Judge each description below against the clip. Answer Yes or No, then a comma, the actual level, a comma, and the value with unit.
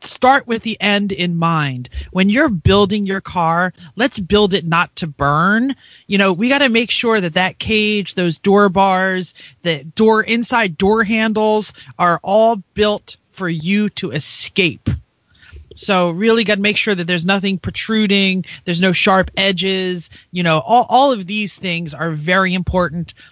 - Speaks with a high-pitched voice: Yes, high, 195 Hz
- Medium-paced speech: Yes, average, 170 wpm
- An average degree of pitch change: Yes, average, 3.5 semitones